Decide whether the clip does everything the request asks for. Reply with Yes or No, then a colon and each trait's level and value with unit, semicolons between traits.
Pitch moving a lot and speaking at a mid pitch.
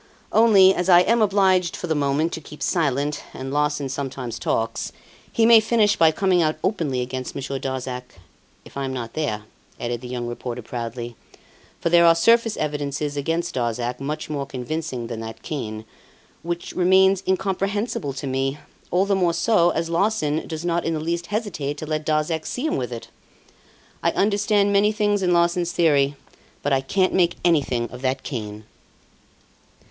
Yes: wide, 5.7 semitones; medium, 155 Hz